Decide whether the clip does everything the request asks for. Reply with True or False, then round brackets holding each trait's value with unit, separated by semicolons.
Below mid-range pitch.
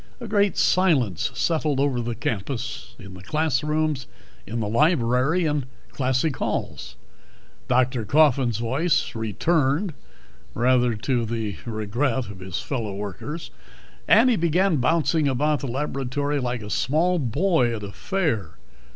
True (130 Hz)